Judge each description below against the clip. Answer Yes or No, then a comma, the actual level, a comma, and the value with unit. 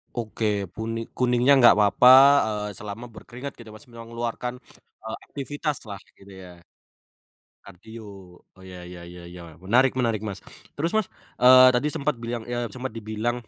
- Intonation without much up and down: No, average, 3.5 semitones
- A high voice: No, low, 115 Hz